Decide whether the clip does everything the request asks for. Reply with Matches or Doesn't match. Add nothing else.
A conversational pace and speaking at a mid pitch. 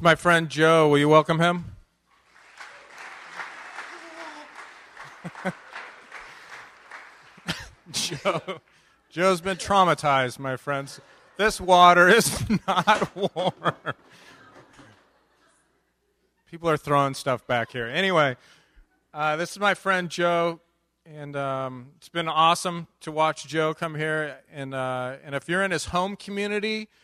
Doesn't match